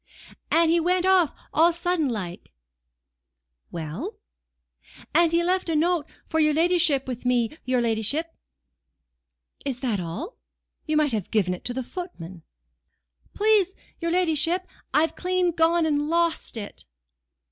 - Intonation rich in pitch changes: Yes, wide, 5.8 semitones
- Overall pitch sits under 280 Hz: No, very high, 320 Hz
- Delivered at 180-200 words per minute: No, average, 145 wpm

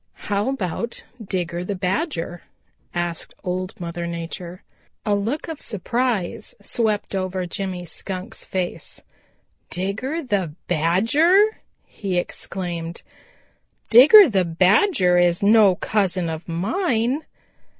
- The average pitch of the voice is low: No, high, 190 Hz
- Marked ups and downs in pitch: No, average, 4.5 semitones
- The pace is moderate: No, slow, 105 wpm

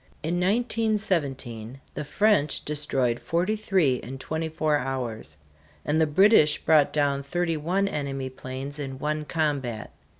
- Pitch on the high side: No, medium, 150 Hz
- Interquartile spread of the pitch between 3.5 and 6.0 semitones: Yes, average, 4.3 semitones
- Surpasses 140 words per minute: No, slow, 135 wpm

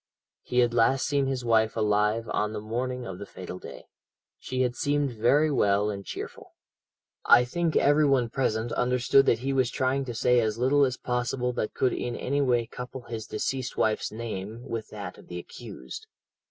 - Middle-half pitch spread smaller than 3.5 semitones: Yes, average, 3.0 semitones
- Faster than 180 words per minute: Yes, average, 190 wpm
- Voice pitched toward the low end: Yes, low, 120 Hz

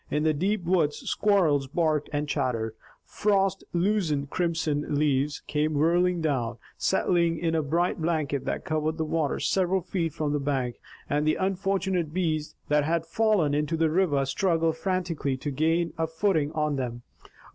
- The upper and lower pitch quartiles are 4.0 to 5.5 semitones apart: No, average, 3.2 semitones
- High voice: No, medium, 160 Hz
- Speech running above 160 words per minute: No, average, 155 wpm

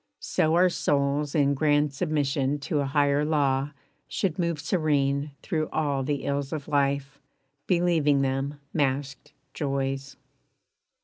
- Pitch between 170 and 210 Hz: No, medium, 145 Hz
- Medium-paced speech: No, slow, 125 wpm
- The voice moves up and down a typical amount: No, narrow, 1.8 semitones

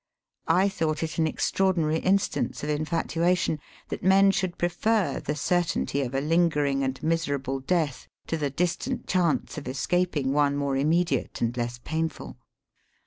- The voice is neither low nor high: Yes, medium, 160 Hz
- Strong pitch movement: No, average, 3.8 semitones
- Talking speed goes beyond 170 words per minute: No, average, 150 wpm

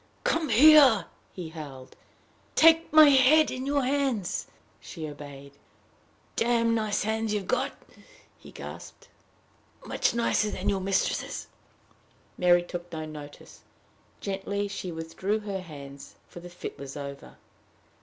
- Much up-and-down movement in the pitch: Yes, wide, 6.7 semitones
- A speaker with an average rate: No, slow, 125 wpm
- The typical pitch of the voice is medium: No, high, 195 Hz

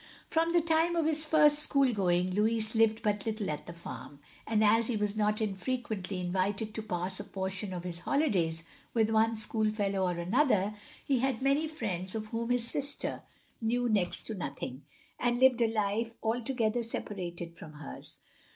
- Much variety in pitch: No, average, 4.3 semitones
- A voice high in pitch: Yes, high, 215 Hz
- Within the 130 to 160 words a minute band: No, average, 175 wpm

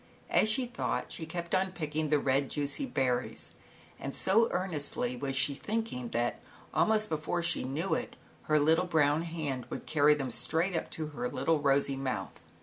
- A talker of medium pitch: Yes, medium, 150 Hz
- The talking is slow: No, average, 175 wpm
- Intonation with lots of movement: No, average, 4.0 semitones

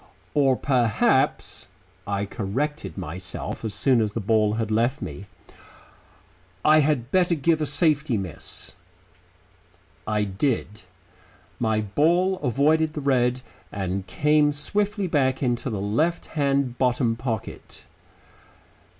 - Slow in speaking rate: Yes, slow, 115 wpm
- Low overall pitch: Yes, low, 125 Hz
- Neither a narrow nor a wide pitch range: No, wide, 5.7 semitones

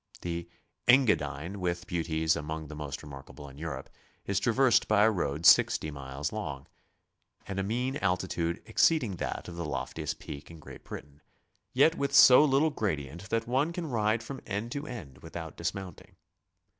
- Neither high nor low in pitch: No, very low, 90 Hz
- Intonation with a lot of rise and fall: Yes, wide, 7.0 semitones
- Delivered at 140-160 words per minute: No, average, 170 wpm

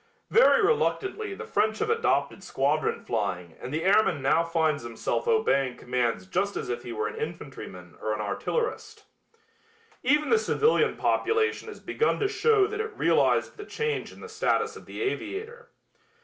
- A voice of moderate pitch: No, high, 220 Hz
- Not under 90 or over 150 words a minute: No, average, 165 wpm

